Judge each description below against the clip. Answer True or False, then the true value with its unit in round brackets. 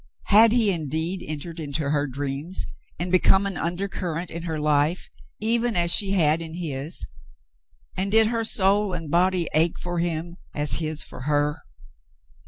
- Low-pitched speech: False (170 Hz)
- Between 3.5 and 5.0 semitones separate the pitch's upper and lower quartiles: True (4.0 semitones)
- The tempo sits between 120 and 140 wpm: False (160 wpm)